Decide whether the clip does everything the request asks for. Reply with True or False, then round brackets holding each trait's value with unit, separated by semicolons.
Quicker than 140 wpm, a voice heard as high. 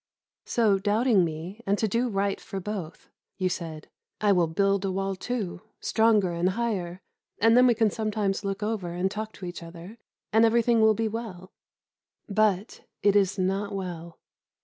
True (170 wpm; 200 Hz)